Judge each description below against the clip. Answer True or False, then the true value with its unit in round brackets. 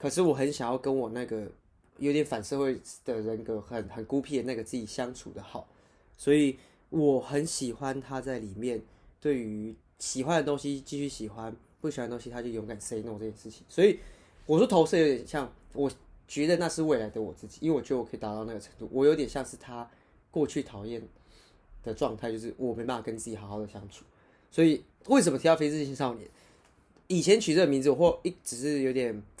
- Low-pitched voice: True (125 Hz)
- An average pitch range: True (4.4 semitones)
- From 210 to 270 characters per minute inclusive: False (320 characters per minute)